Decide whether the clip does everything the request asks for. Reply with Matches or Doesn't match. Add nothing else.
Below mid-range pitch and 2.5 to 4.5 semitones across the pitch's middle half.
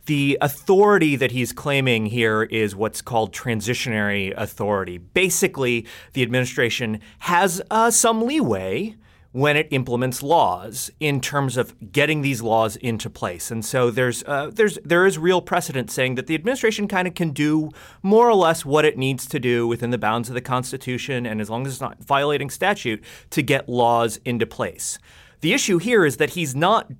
Doesn't match